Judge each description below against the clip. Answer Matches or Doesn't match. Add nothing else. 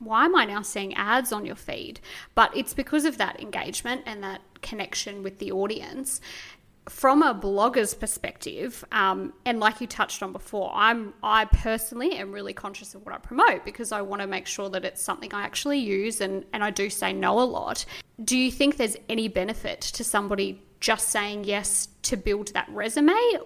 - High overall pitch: Matches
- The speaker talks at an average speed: Matches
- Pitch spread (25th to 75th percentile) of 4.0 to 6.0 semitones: Doesn't match